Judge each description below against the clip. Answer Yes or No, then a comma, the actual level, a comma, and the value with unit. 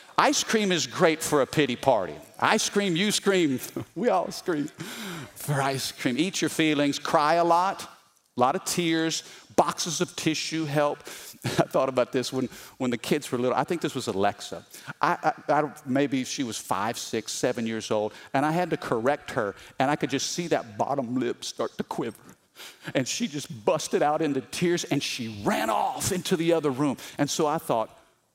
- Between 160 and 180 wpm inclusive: No, average, 200 wpm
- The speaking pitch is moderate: Yes, medium, 150 Hz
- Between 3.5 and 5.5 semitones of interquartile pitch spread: Yes, average, 4.4 semitones